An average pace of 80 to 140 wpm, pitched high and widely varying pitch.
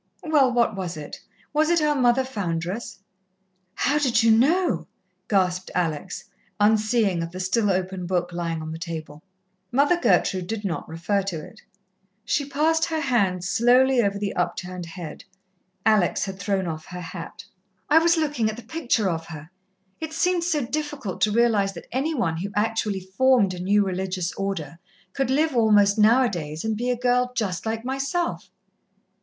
No: average, 170 wpm; high, 210 Hz; wide, 6.2 semitones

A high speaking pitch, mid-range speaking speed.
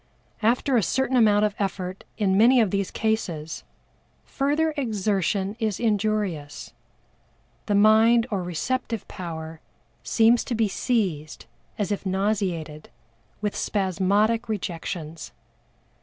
No: high, 205 Hz; slow, 110 wpm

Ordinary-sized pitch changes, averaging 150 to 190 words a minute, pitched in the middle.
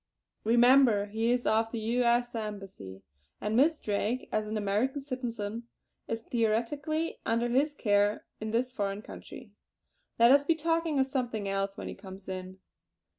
No: average, 3.7 semitones; average, 160 wpm; high, 230 Hz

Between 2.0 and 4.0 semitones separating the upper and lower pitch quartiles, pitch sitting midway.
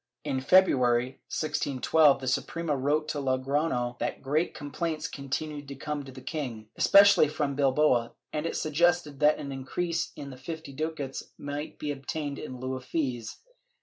Yes: average, 2.8 semitones; medium, 145 Hz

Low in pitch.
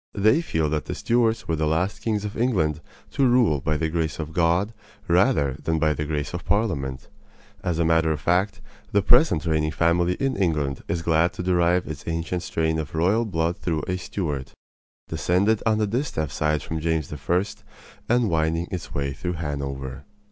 Yes: very low, 85 Hz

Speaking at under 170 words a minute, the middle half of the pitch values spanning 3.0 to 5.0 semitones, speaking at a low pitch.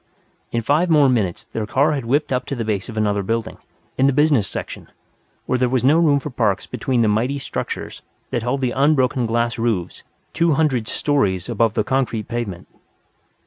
No: average, 190 wpm; average, 3.9 semitones; low, 125 Hz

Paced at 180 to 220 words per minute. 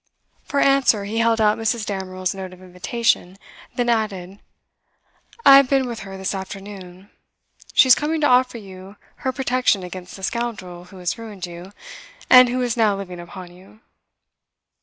No: average, 165 wpm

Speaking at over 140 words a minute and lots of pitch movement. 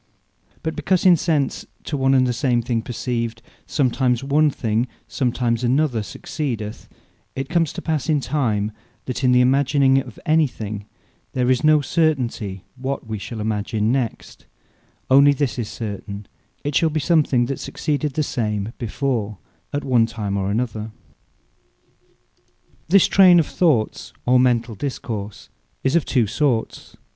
No: average, 160 wpm; average, 4.3 semitones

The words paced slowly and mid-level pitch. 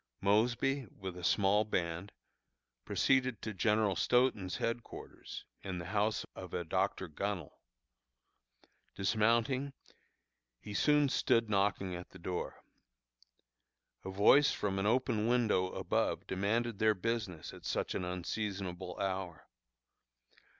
No: slow, 115 wpm; low, 100 Hz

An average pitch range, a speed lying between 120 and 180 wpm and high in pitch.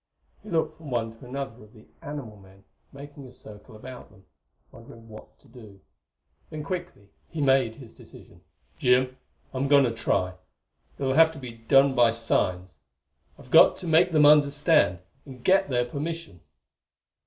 No: average, 4.4 semitones; average, 165 wpm; low, 130 Hz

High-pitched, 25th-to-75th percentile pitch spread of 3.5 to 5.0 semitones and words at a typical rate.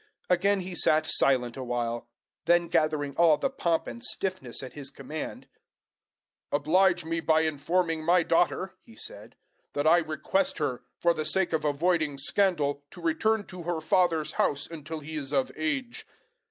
No: medium, 160 Hz; average, 3.8 semitones; average, 165 wpm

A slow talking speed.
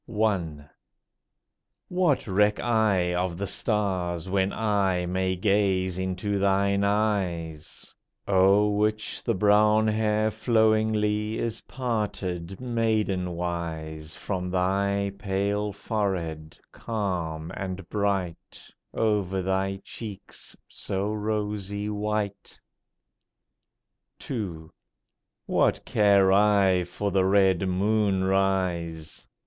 Yes: slow, 95 wpm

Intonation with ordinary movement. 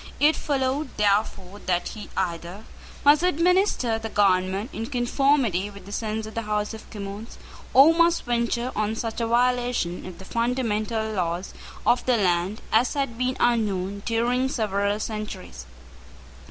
Yes: average, 3.8 semitones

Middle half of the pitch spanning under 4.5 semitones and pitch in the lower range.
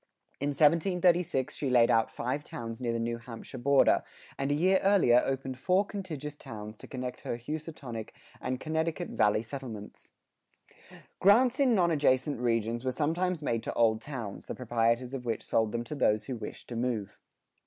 No: average, 5.1 semitones; low, 130 Hz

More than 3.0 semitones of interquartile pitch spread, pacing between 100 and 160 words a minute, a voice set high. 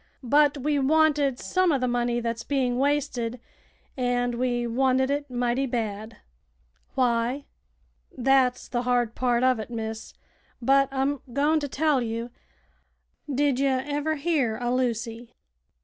No: average, 2.7 semitones; slow, 135 wpm; very high, 255 Hz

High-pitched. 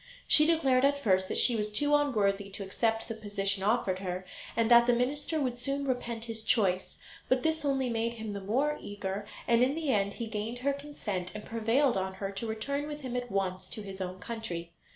Yes: high, 225 Hz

